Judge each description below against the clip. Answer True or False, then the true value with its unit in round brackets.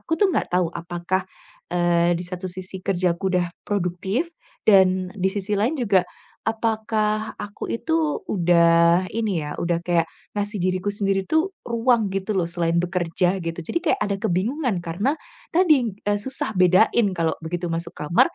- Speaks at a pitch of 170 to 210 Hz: True (190 Hz)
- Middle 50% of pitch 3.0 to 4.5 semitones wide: True (3.8 semitones)